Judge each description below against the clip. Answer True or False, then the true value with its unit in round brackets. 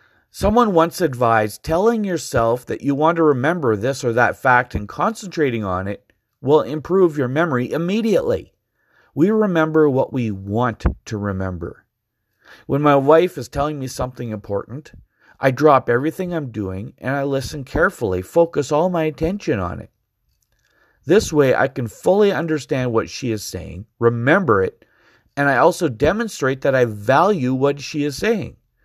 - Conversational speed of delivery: True (160 wpm)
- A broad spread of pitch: True (5.7 semitones)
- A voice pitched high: False (140 Hz)